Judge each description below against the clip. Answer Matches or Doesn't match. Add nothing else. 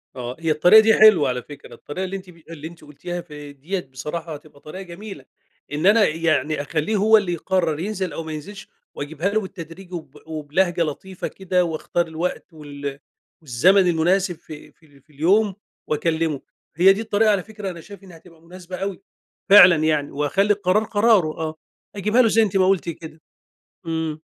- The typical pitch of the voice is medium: Matches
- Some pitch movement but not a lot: Matches